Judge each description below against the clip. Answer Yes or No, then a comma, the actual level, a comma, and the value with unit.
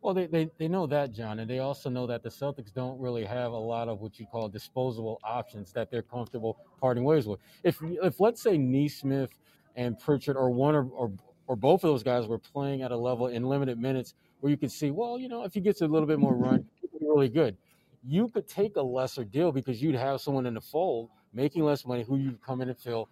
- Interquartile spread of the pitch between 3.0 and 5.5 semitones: Yes, average, 3.9 semitones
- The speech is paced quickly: Yes, fast, 245 wpm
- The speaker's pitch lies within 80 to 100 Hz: No, low, 130 Hz